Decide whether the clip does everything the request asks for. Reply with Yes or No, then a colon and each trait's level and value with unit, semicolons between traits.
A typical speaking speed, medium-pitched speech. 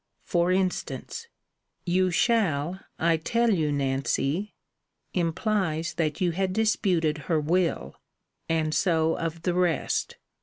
No: slow, 115 wpm; medium, 170 Hz